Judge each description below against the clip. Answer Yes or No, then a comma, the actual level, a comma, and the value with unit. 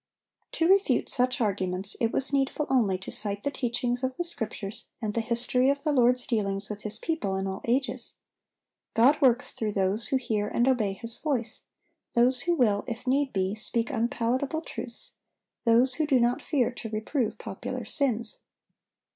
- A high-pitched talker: Yes, high, 240 Hz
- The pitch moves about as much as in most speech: Yes, average, 3.8 semitones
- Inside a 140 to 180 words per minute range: Yes, average, 175 wpm